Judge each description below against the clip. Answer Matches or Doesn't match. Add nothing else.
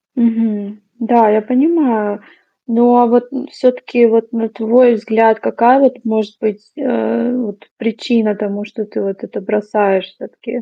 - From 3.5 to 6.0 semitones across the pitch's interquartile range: Doesn't match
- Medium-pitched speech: Doesn't match